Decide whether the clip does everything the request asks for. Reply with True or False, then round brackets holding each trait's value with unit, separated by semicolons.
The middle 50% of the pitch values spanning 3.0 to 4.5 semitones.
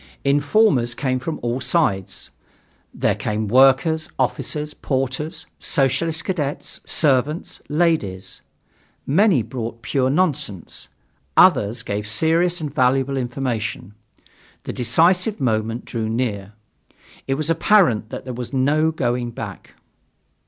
False (5.0 semitones)